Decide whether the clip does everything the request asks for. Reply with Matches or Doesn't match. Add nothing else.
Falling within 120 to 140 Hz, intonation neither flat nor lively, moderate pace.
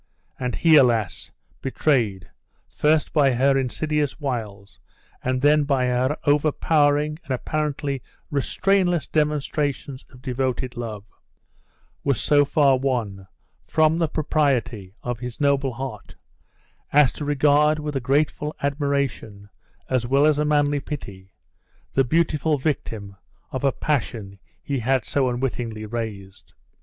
Doesn't match